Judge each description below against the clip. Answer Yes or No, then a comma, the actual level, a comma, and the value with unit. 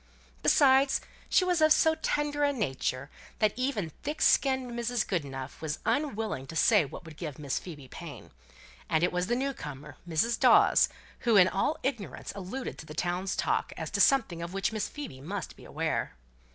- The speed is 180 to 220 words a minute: Yes, average, 185 wpm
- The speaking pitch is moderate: No, high, 200 Hz